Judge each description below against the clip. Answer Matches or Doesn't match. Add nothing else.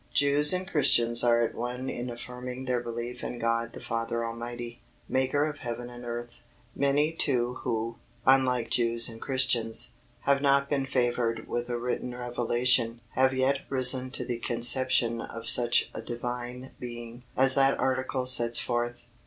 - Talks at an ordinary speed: Matches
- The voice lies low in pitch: Matches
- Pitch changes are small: Matches